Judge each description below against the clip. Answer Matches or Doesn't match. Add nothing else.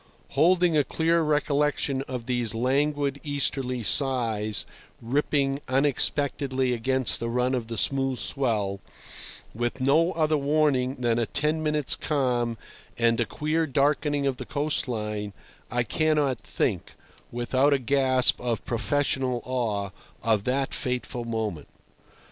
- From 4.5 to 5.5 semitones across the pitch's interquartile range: Doesn't match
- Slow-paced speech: Matches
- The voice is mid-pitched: Doesn't match